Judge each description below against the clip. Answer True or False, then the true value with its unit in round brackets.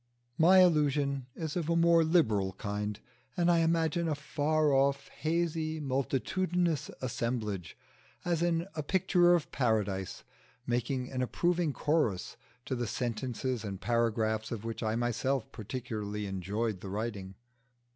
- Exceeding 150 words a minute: False (135 wpm)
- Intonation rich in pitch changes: True (6.7 semitones)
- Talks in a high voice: False (130 Hz)